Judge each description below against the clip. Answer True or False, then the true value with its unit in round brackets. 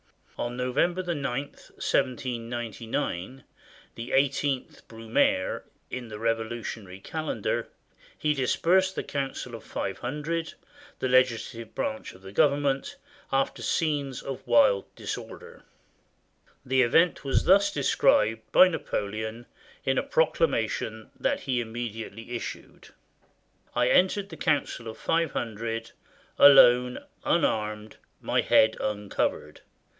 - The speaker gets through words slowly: True (120 wpm)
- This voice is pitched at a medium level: False (125 Hz)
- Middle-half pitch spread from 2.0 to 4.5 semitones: True (4.2 semitones)